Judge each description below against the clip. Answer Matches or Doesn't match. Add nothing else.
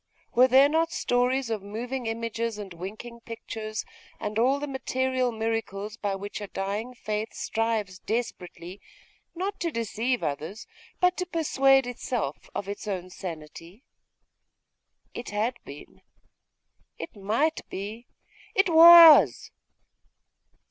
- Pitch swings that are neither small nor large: Matches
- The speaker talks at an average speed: Doesn't match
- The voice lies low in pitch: Doesn't match